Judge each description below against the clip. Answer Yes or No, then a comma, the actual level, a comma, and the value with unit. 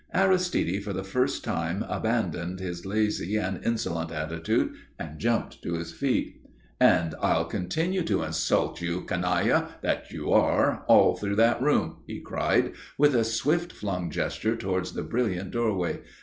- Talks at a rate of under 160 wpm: Yes, average, 150 wpm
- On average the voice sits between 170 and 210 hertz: No, very low, 95 Hz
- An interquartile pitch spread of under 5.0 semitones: No, wide, 5.5 semitones